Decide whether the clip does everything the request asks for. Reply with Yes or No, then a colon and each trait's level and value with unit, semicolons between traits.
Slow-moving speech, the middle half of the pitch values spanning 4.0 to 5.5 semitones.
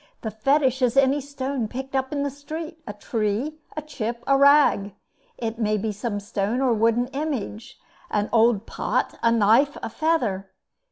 No: average, 170 wpm; average, 4.6 semitones